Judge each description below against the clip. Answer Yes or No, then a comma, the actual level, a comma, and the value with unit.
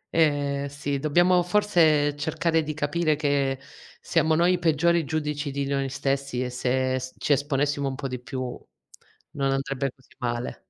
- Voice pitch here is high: No, medium, 145 Hz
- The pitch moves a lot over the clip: No, narrow, 2.5 semitones